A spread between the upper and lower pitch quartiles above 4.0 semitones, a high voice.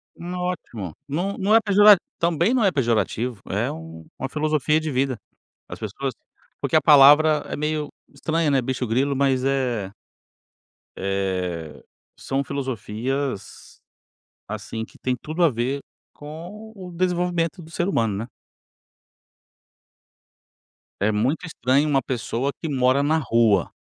No: wide, 5.6 semitones; medium, 140 Hz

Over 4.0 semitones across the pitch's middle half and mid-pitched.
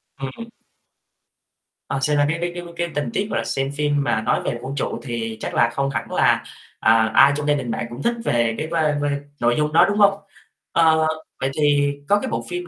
Yes: average, 5.0 semitones; medium, 145 Hz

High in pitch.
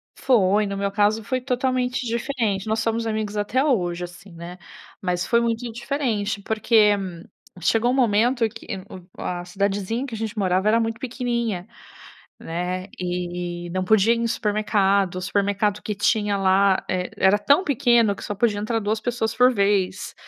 Yes: high, 210 Hz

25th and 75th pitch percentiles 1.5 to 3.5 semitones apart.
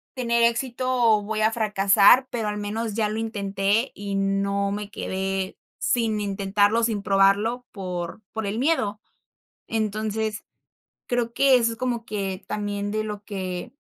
Yes: narrow, 2.5 semitones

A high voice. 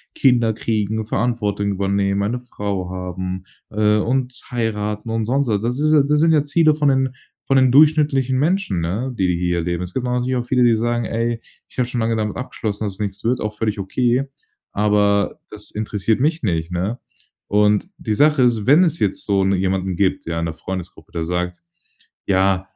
No: low, 110 Hz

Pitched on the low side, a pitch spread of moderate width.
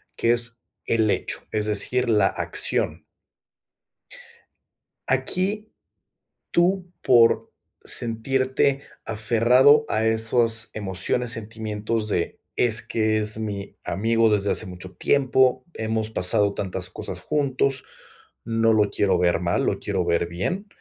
Yes: low, 110 Hz; average, 3.3 semitones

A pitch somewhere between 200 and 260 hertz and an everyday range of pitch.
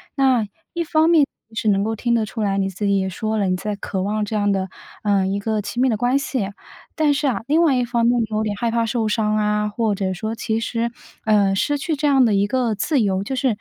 Yes: high, 220 Hz; average, 3.6 semitones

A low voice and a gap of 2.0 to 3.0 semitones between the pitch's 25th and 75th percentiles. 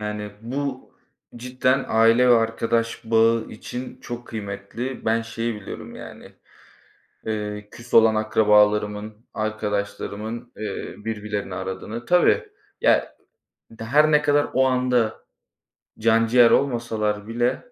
Yes: low, 115 Hz; narrow, 2.5 semitones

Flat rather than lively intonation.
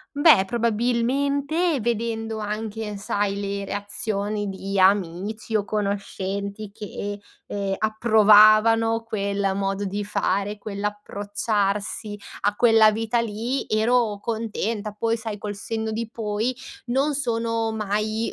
Yes: narrow, 2.0 semitones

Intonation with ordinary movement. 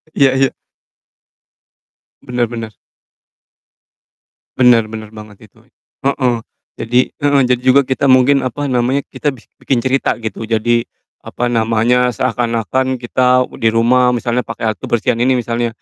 No: narrow, 2.1 semitones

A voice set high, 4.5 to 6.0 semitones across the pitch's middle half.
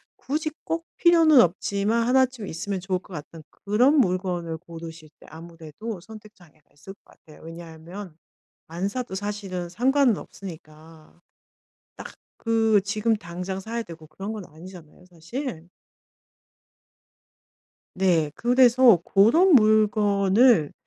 Yes: high, 195 Hz; average, 5.3 semitones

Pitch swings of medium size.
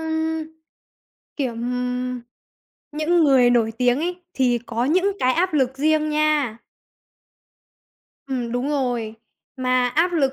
Yes: average, 3.8 semitones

